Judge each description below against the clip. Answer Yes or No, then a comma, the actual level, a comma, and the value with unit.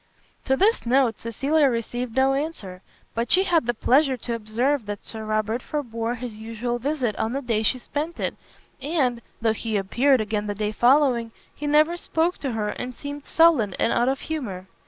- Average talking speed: Yes, average, 190 wpm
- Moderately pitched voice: No, high, 245 Hz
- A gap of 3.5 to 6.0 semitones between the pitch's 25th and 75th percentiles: Yes, average, 4.5 semitones